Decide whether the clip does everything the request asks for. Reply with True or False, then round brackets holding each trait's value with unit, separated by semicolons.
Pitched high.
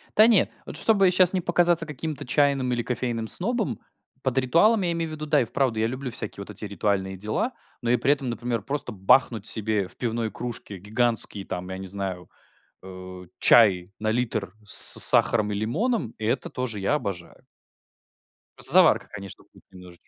False (115 Hz)